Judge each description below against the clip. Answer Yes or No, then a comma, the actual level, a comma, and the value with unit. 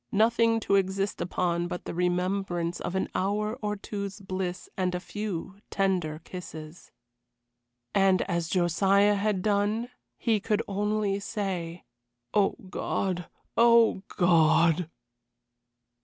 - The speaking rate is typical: No, slow, 115 wpm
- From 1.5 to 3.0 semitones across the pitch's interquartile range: Yes, average, 2.7 semitones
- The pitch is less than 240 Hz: Yes, high, 190 Hz